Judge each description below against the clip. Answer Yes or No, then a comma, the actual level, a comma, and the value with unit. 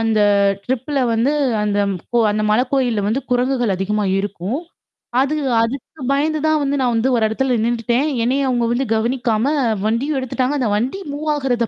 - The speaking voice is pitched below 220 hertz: No, high, 245 Hz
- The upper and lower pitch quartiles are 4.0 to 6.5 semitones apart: No, average, 3.4 semitones